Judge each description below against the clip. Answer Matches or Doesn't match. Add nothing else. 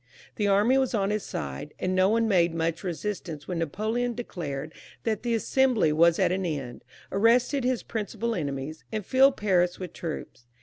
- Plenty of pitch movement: Matches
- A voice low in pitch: Doesn't match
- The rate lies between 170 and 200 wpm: Matches